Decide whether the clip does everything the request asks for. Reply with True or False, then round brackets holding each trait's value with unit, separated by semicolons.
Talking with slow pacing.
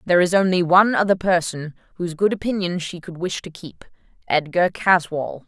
False (165 wpm)